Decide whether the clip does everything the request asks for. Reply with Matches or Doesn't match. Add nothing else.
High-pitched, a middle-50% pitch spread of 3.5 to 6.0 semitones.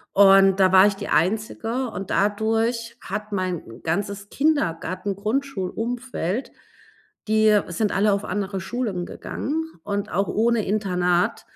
Doesn't match